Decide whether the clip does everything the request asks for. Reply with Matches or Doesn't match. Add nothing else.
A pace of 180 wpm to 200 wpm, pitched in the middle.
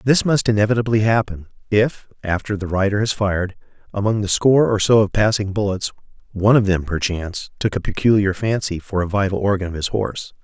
Doesn't match